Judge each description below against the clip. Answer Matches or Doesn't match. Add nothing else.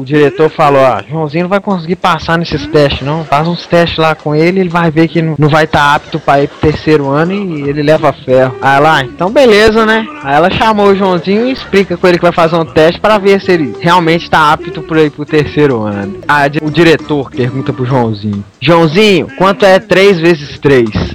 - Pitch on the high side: Doesn't match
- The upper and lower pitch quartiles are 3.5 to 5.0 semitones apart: Matches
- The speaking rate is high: Matches